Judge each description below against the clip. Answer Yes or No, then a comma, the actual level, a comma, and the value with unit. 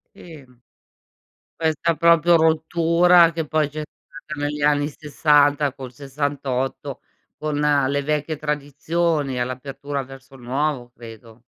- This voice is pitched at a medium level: Yes, medium, 145 Hz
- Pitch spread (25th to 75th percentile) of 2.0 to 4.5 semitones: Yes, narrow, 2.6 semitones